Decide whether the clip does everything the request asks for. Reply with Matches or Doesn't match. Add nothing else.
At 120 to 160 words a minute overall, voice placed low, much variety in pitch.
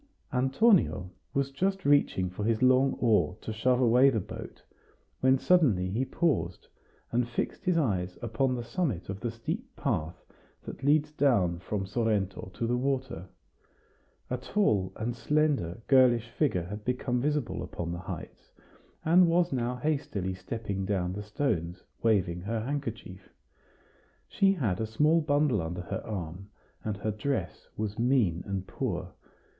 Matches